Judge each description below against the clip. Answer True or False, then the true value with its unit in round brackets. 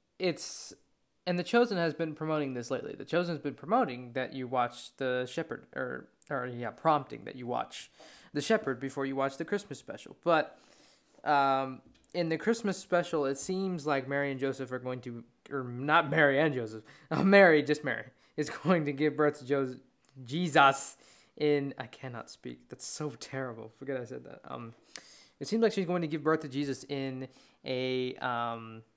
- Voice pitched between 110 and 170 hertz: True (140 Hz)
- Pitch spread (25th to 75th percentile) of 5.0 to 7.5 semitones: False (3.9 semitones)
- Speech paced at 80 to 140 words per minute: False (190 wpm)